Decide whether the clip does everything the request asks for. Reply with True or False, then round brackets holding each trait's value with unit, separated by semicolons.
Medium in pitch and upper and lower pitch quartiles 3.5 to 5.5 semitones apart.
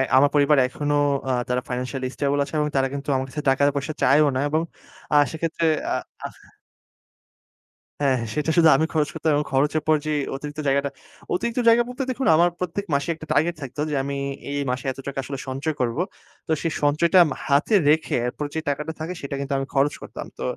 False (145 Hz; 2.5 semitones)